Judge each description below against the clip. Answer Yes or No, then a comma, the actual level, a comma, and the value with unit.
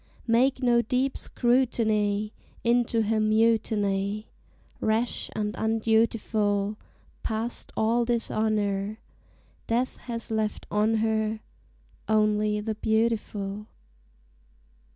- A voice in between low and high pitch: No, high, 220 Hz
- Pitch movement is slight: Yes, narrow, 1.5 semitones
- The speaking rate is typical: No, slow, 85 wpm